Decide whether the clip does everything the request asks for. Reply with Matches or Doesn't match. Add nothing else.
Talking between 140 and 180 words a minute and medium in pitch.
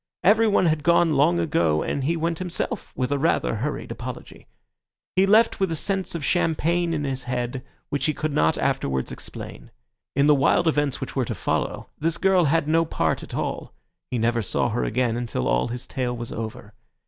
Doesn't match